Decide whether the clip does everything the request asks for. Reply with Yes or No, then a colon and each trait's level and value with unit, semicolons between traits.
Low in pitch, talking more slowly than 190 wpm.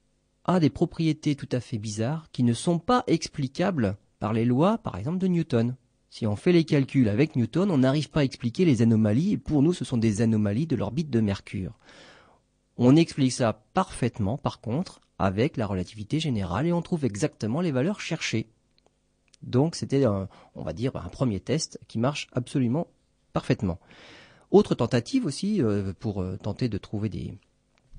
Yes: low, 130 Hz; average, 175 wpm